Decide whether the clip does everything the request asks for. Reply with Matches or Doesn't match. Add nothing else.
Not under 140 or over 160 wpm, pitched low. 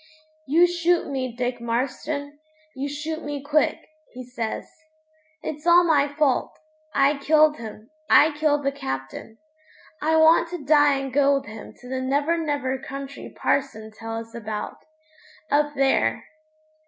Doesn't match